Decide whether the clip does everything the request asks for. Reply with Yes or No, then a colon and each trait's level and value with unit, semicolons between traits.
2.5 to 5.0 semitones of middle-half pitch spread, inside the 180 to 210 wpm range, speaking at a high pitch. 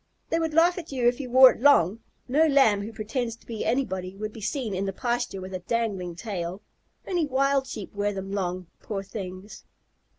No: wide, 5.4 semitones; fast, 205 wpm; high, 220 Hz